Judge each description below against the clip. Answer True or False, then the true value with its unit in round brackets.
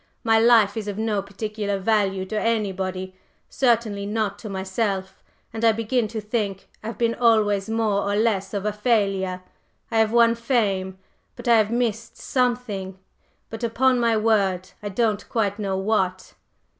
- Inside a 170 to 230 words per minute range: False (160 wpm)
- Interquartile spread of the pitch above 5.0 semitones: False (2.6 semitones)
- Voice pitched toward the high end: True (215 Hz)